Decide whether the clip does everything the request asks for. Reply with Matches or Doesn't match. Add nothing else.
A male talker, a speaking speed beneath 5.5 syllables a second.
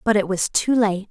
Doesn't match